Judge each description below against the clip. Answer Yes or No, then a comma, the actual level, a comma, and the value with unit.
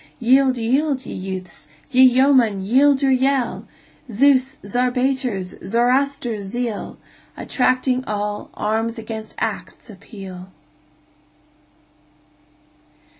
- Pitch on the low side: No, high, 245 Hz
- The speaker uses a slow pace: Yes, slow, 85 wpm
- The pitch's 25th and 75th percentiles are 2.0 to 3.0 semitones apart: No, average, 3.9 semitones